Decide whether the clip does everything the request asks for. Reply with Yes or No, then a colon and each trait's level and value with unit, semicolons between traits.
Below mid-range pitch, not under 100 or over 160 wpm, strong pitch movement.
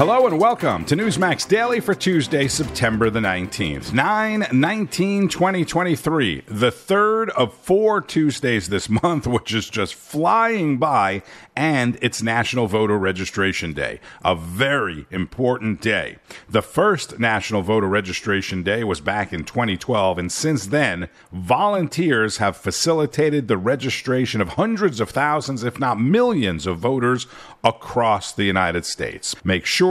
Yes: low, 125 Hz; slow, 135 wpm; wide, 8.3 semitones